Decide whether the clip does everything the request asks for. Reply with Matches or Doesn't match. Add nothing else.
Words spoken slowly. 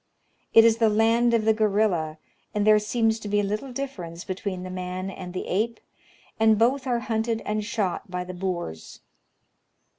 Doesn't match